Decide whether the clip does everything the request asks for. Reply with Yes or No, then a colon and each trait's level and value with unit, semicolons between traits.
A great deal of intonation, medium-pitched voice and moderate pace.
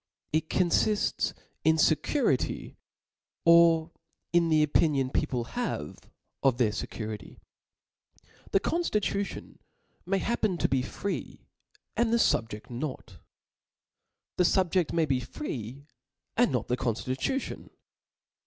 No: wide, 7.2 semitones; medium, 160 Hz; slow, 110 wpm